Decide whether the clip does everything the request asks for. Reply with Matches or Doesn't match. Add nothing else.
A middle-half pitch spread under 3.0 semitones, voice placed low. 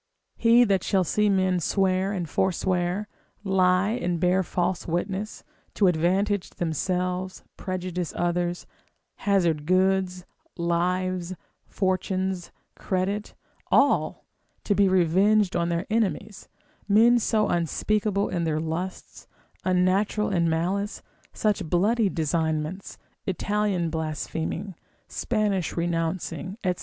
Doesn't match